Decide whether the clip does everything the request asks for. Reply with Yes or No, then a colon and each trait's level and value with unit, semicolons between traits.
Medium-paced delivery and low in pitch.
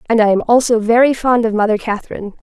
No: average, 195 wpm; high, 225 Hz